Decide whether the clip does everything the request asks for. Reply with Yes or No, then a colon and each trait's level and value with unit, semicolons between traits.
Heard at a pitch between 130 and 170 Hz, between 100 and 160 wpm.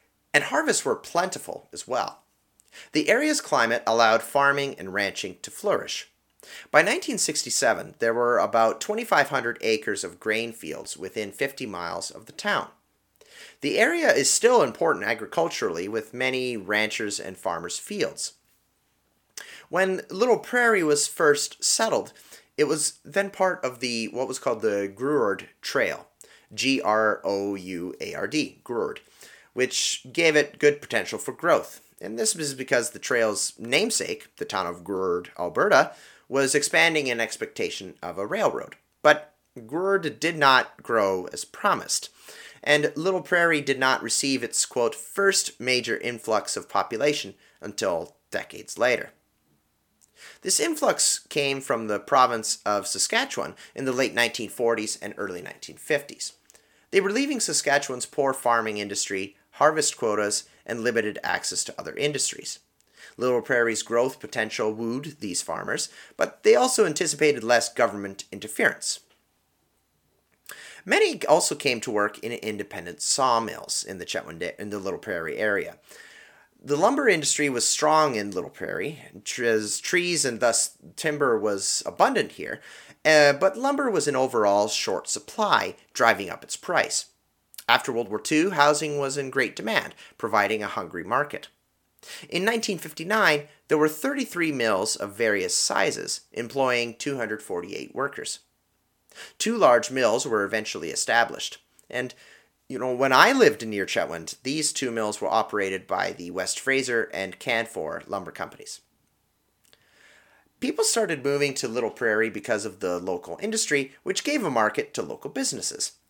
Yes: low, 135 Hz; average, 145 wpm